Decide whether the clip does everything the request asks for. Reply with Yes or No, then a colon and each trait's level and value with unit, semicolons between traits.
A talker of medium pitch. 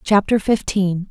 No: high, 195 Hz